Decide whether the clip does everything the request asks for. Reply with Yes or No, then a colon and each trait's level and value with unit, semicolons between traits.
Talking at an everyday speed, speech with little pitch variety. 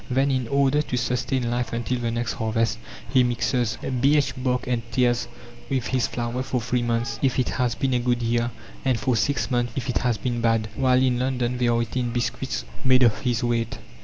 No: fast, 210 wpm; narrow, 1.5 semitones